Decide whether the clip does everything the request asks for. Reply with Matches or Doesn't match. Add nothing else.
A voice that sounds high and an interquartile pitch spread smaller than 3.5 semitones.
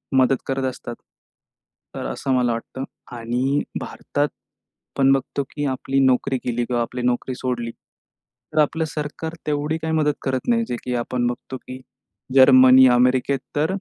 Doesn't match